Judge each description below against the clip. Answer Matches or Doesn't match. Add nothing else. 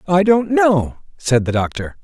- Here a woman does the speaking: Doesn't match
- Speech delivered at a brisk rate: Doesn't match